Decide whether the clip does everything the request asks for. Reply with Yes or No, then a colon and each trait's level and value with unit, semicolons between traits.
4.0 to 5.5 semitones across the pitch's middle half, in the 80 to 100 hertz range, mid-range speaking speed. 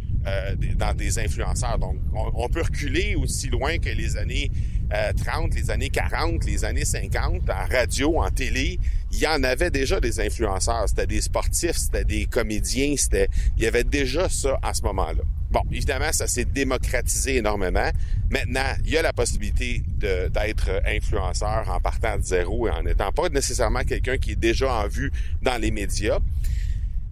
Yes: average, 4.4 semitones; very low, 90 Hz; average, 180 wpm